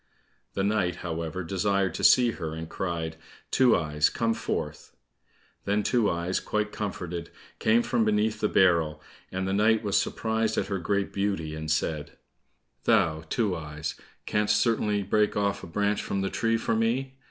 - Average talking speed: Yes, average, 165 wpm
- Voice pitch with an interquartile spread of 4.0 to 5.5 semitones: Yes, average, 4.4 semitones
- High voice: No, low, 100 Hz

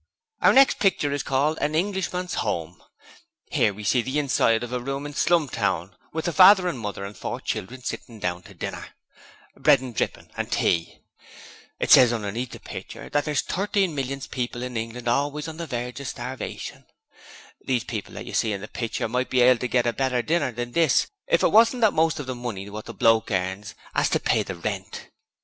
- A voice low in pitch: Yes, low, 125 Hz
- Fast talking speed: Yes, fast, 210 wpm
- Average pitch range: Yes, average, 5.0 semitones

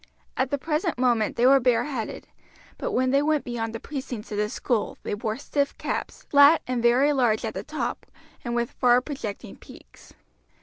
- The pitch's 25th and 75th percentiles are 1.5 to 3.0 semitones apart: No, average, 3.5 semitones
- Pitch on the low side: No, very high, 250 Hz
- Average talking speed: Yes, average, 185 wpm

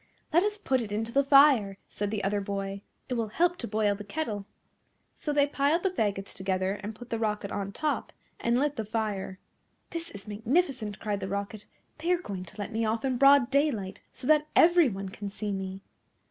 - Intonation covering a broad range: Yes, wide, 5.8 semitones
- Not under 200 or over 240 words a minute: Yes, fast, 205 wpm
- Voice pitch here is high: Yes, high, 220 Hz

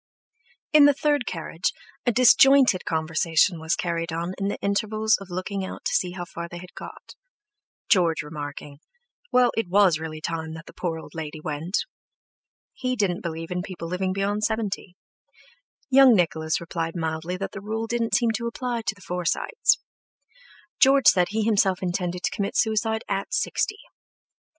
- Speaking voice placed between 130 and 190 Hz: Yes, medium, 185 Hz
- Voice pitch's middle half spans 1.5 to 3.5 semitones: No, average, 4.9 semitones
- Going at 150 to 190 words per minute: Yes, average, 165 wpm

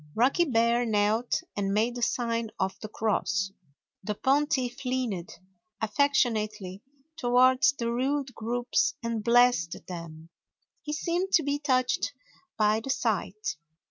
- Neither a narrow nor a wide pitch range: Yes, average, 3.5 semitones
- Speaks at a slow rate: Yes, slow, 125 wpm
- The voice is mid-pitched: No, high, 235 Hz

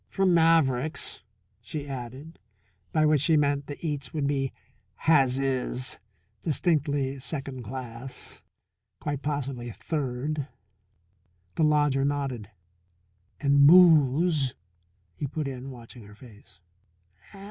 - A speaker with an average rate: No, slow, 105 wpm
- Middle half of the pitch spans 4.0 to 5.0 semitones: No, average, 2.8 semitones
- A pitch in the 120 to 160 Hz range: Yes, medium, 140 Hz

